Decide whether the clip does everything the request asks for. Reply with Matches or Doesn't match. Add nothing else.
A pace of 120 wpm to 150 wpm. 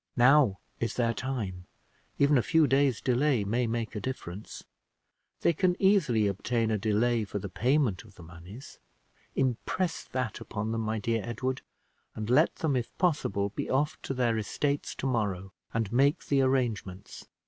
Doesn't match